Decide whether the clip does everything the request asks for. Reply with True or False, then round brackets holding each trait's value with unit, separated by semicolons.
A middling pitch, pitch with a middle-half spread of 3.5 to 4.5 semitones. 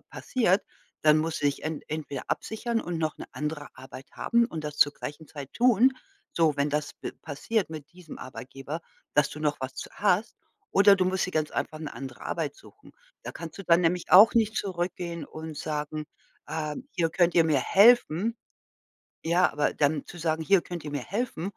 True (160 Hz; 3.8 semitones)